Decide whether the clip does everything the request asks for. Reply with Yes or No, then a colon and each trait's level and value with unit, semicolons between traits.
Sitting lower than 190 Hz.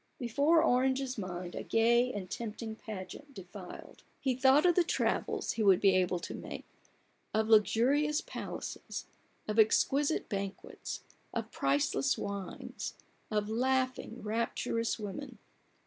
No: high, 225 Hz